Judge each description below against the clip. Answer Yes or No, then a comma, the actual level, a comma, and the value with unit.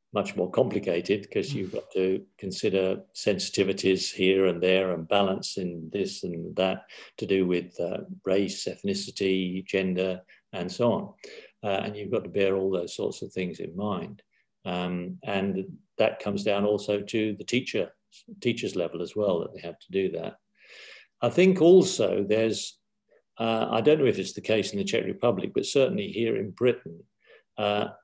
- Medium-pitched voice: No, very low, 95 Hz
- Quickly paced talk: Yes, fast, 175 wpm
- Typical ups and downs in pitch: Yes, average, 3.1 semitones